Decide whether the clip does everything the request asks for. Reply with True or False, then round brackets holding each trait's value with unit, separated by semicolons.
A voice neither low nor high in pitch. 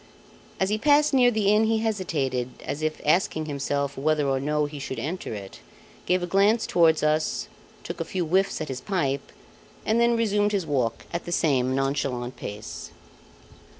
True (155 Hz)